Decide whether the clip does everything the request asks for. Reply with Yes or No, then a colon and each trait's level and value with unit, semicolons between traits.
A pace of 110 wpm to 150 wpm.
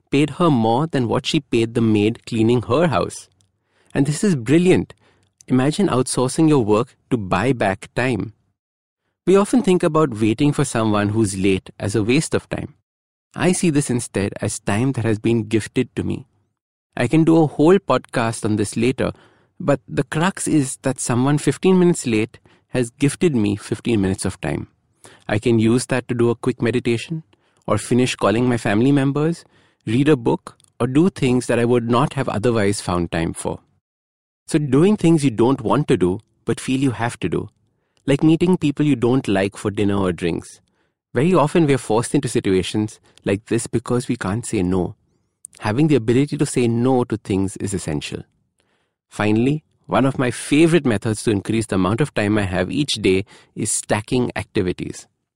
No: average, 185 wpm